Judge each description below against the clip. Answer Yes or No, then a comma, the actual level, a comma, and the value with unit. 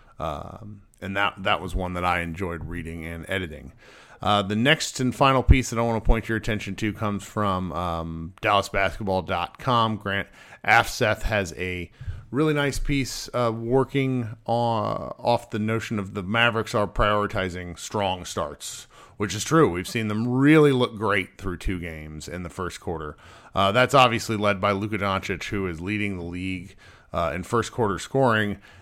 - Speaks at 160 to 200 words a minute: Yes, average, 175 wpm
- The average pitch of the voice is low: Yes, low, 105 Hz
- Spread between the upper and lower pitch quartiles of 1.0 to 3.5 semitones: No, average, 3.9 semitones